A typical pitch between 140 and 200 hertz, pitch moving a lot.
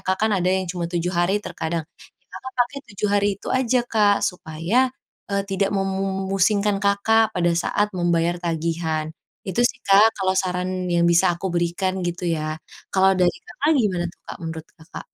No: high, 190 Hz; average, 2.8 semitones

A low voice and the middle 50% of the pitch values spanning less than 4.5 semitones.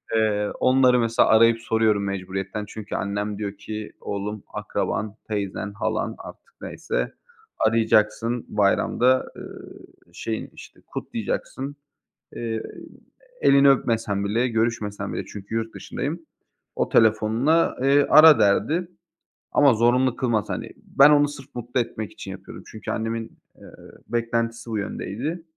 Yes: low, 115 Hz; average, 3.4 semitones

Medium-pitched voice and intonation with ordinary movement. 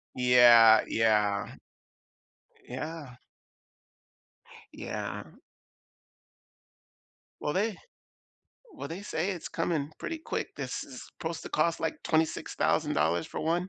No: medium, 155 Hz; wide, 6.1 semitones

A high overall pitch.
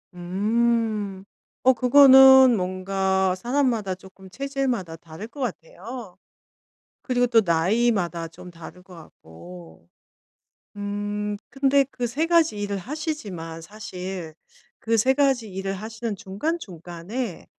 Yes: high, 205 Hz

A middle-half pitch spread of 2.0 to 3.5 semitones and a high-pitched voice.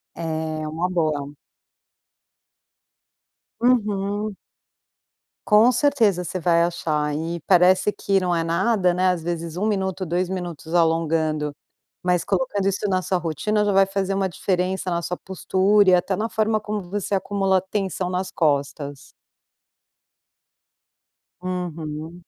No: average, 2.9 semitones; medium, 180 Hz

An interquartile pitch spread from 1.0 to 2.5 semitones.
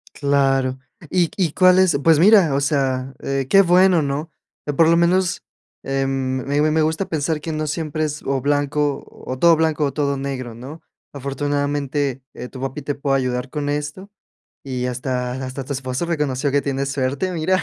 No: average, 2.9 semitones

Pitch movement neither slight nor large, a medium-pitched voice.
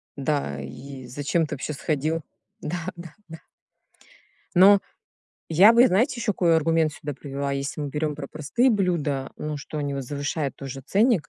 Yes: average, 3.5 semitones; medium, 150 Hz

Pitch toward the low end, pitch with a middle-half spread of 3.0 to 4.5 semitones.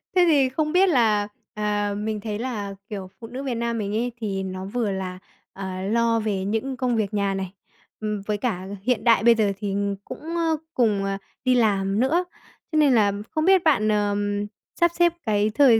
No: high, 220 Hz; average, 4.0 semitones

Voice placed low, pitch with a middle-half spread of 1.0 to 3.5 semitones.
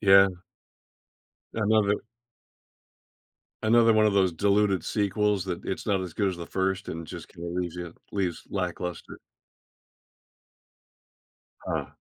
Yes: very low, 95 Hz; average, 2.7 semitones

